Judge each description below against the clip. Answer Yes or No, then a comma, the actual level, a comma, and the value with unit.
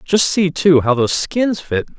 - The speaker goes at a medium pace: No, fast, 210 wpm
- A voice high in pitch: No, medium, 160 Hz